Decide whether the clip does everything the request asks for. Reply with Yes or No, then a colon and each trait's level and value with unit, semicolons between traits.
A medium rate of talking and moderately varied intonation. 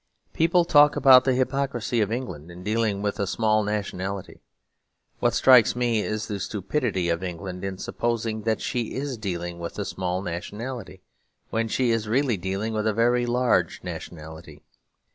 Yes: average, 160 wpm; average, 4.5 semitones